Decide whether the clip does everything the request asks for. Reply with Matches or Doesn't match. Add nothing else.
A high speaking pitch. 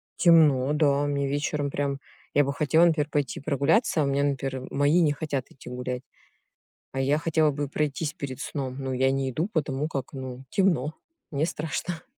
Doesn't match